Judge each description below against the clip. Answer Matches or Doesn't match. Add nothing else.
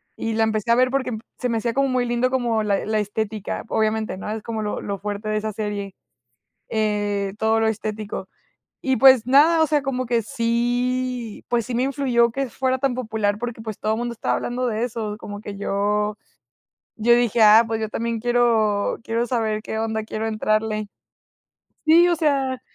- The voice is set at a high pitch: Matches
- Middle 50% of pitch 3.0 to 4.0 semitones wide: Doesn't match